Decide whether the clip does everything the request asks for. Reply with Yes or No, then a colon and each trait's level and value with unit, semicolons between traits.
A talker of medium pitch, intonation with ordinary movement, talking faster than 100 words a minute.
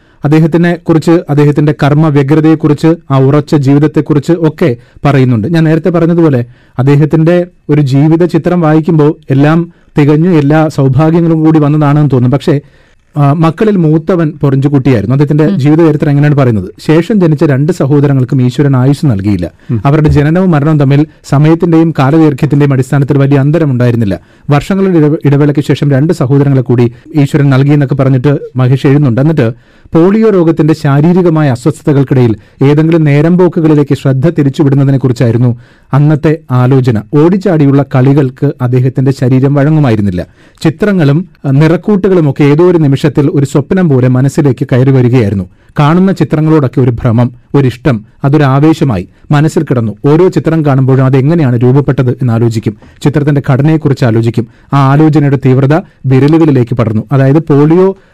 Yes: medium, 145 Hz; average, 3.0 semitones; average, 120 wpm